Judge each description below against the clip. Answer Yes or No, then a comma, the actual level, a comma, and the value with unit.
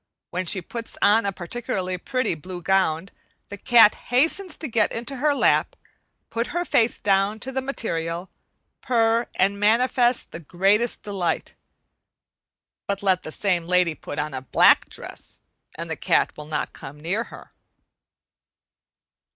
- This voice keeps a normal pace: Yes, average, 150 wpm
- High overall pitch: Yes, high, 200 Hz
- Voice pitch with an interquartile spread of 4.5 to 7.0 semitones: Yes, average, 5.1 semitones